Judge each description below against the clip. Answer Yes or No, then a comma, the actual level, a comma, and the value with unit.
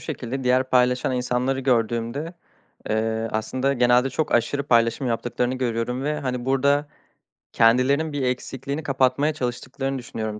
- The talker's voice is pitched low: Yes, low, 130 Hz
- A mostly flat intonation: Yes, narrow, 2.2 semitones